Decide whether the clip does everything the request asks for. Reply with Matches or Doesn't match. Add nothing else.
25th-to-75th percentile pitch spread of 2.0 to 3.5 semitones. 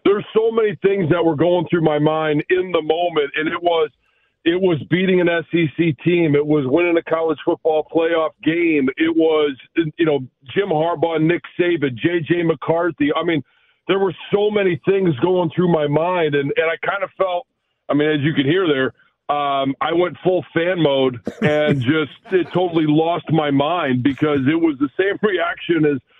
Matches